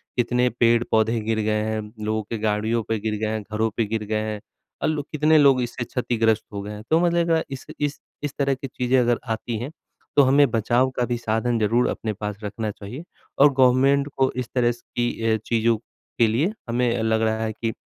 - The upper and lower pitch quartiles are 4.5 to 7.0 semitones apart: No, average, 2.9 semitones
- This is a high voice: No, low, 115 Hz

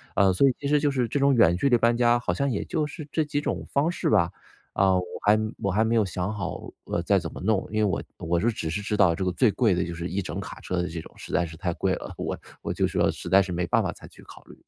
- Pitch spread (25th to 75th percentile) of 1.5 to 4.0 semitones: No, wide, 5.6 semitones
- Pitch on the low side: Yes, low, 100 Hz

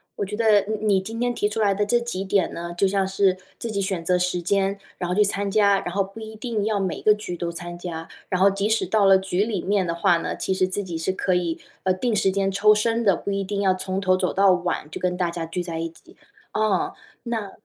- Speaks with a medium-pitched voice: No, high, 195 Hz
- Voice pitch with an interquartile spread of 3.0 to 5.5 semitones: No, narrow, 2.4 semitones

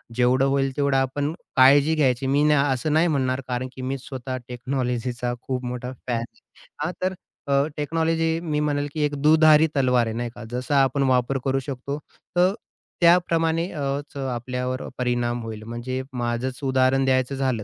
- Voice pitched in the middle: No, low, 130 Hz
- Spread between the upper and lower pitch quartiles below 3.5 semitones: Yes, average, 2.8 semitones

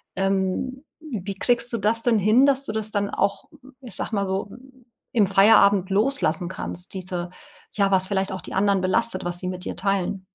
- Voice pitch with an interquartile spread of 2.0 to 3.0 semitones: Yes, narrow, 2.6 semitones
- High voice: Yes, high, 200 Hz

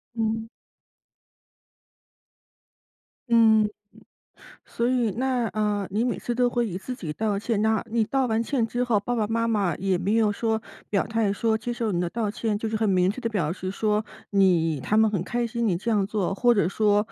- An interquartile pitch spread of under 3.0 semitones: Yes, narrow, 2.6 semitones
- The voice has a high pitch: Yes, high, 220 Hz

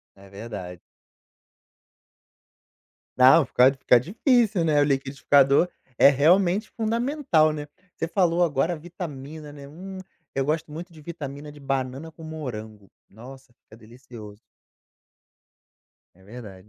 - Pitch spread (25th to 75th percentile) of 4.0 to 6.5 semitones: Yes, average, 4.8 semitones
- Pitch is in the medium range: Yes, medium, 145 Hz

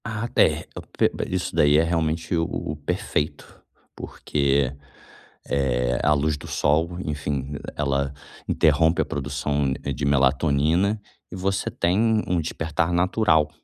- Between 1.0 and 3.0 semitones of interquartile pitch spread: No, average, 3.5 semitones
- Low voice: Yes, very low, 75 Hz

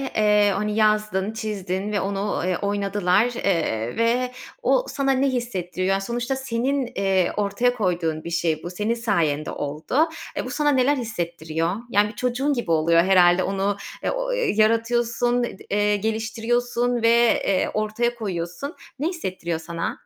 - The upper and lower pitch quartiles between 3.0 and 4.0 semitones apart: No, average, 4.7 semitones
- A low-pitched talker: No, high, 210 Hz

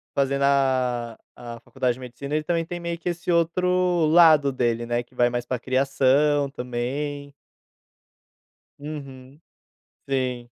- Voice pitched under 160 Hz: Yes, medium, 140 Hz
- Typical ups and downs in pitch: Yes, average, 3.6 semitones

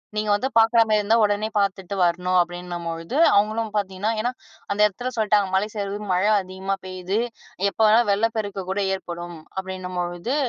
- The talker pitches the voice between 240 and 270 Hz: No, high, 200 Hz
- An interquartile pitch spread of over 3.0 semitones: No, average, 2.7 semitones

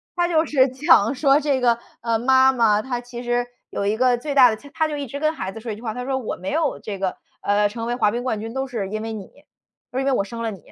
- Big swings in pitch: No, average, 3.4 semitones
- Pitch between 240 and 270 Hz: Yes, high, 245 Hz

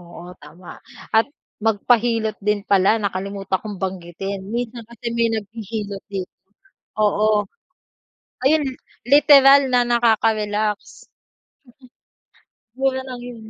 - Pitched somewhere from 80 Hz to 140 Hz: No, high, 215 Hz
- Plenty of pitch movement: No, average, 3.3 semitones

